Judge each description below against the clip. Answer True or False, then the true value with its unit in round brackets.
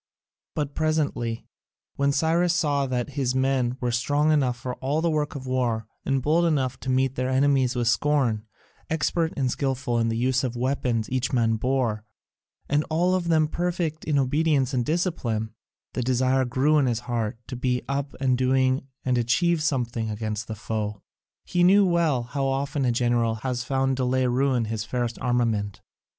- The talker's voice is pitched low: True (130 Hz)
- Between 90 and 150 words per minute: False (180 wpm)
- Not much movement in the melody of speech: False (3.3 semitones)